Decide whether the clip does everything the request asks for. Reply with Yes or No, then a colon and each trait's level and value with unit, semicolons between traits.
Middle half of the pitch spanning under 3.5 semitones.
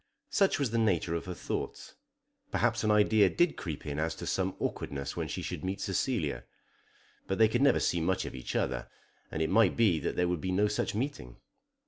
No: average, 5.0 semitones